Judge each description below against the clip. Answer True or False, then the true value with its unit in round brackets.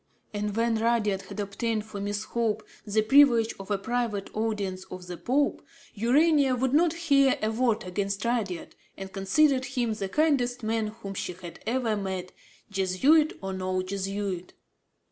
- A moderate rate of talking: True (160 wpm)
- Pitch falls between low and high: False (215 Hz)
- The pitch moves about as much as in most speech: True (4.0 semitones)